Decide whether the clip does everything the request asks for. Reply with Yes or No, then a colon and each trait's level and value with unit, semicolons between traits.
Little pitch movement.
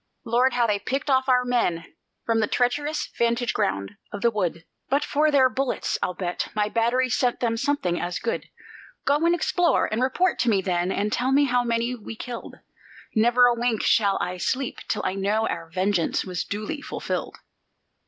No: average, 4.2 semitones